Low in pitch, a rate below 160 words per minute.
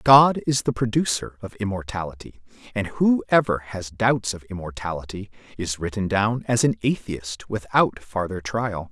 Yes: low, 105 Hz; average, 140 wpm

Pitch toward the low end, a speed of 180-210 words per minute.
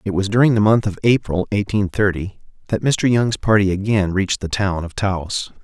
Yes: low, 100 Hz; average, 200 wpm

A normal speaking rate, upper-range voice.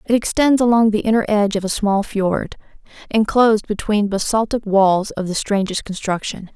Yes: average, 165 wpm; high, 210 Hz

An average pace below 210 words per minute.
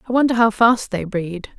No: fast, 225 wpm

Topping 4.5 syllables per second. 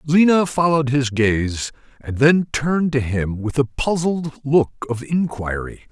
No: 4.1 syllables/s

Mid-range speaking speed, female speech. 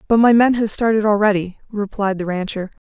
Yes: average, 190 wpm; female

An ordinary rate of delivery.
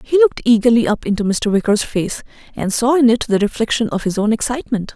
No: fast, 220 wpm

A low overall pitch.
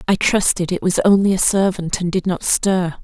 No: medium, 185 Hz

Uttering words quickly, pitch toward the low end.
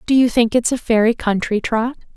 No: fast, 220 wpm; high, 230 Hz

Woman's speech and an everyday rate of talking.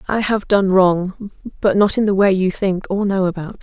No: female; fast, 230 wpm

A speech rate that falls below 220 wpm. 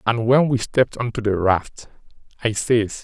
Yes: average, 200 wpm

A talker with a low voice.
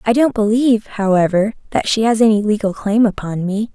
No: high, 215 Hz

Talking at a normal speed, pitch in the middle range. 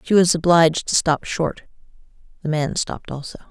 Yes: average, 170 wpm; medium, 165 Hz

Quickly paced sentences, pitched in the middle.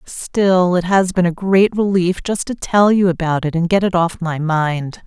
Yes: fast, 225 wpm; medium, 180 Hz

